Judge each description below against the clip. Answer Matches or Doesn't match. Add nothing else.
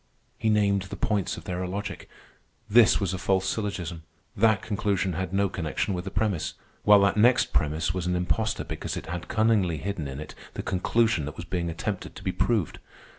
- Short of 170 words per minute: Doesn't match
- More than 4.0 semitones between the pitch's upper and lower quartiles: Doesn't match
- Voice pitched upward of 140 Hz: Doesn't match